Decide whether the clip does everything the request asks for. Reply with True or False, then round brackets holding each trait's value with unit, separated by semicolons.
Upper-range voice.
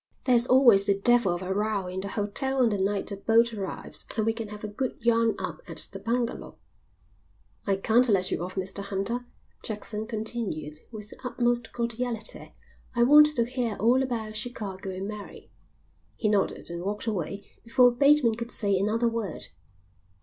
True (220 Hz)